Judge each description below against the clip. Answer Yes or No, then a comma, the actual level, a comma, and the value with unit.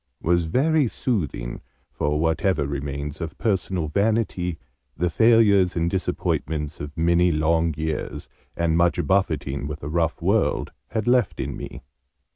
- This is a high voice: No, very low, 85 Hz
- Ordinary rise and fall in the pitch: Yes, average, 4.3 semitones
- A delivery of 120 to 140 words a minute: Yes, slow, 135 wpm